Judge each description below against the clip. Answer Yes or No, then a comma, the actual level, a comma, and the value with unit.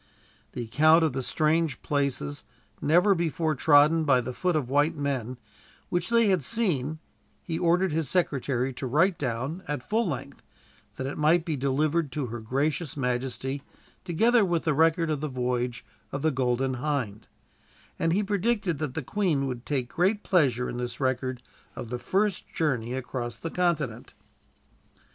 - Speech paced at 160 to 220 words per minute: Yes, average, 165 wpm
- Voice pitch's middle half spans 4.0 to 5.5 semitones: Yes, average, 4.7 semitones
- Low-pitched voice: No, medium, 145 Hz